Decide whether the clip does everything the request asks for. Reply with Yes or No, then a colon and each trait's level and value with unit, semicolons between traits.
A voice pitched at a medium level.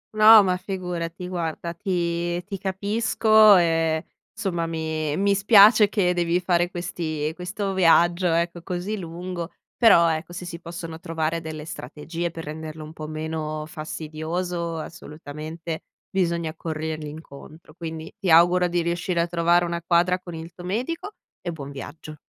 Yes: medium, 170 Hz